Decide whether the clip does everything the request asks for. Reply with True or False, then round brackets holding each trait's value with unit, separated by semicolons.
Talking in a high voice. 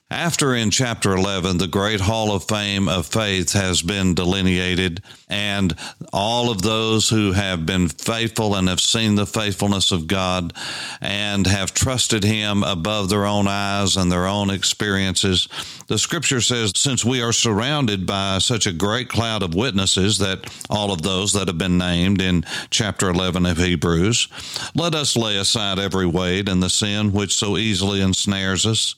False (100 Hz)